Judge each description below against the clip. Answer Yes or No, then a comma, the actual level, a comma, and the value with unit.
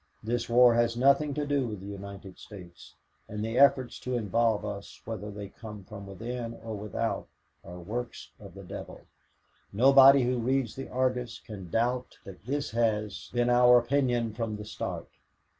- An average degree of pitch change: Yes, average, 3.0 semitones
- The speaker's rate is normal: Yes, average, 170 wpm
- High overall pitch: No, low, 115 Hz